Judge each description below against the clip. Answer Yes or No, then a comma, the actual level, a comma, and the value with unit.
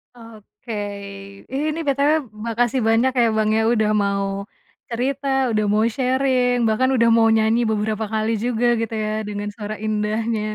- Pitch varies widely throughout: No, narrow, 2.5 semitones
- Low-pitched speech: No, high, 225 Hz